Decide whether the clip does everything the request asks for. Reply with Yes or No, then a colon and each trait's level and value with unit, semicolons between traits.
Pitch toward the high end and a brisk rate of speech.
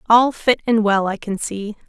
Yes: high, 215 Hz; fast, 225 wpm